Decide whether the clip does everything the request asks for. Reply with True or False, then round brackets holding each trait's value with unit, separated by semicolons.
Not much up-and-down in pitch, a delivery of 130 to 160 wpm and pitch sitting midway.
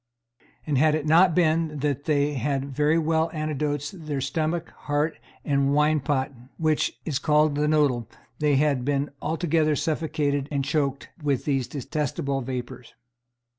True (1.9 semitones; 145 wpm; 150 Hz)